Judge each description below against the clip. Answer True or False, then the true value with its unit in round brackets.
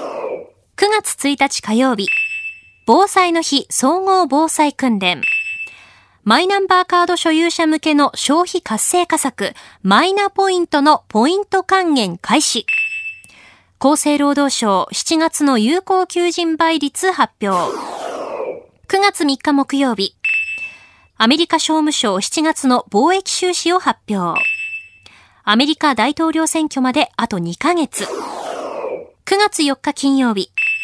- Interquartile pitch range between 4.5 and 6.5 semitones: False (8.4 semitones)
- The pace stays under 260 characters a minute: True (210 characters per minute)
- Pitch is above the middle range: True (295 Hz)